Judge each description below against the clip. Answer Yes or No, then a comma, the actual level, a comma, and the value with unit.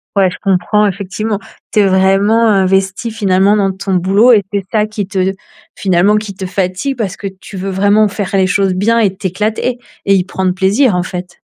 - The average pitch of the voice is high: Yes, high, 195 Hz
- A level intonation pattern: Yes, narrow, 2.0 semitones